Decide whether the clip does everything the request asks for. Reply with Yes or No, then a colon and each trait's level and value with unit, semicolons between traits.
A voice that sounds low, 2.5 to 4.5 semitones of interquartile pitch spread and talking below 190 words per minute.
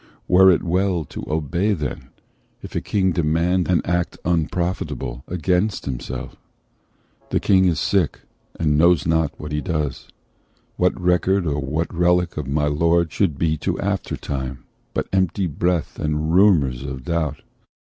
Yes: very low, 85 Hz; average, 3.3 semitones; average, 150 wpm